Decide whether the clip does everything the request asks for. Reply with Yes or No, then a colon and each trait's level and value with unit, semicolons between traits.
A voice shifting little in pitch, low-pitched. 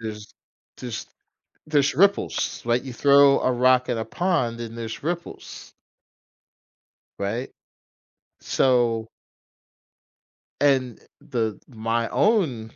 No: average, 3.6 semitones; low, 125 Hz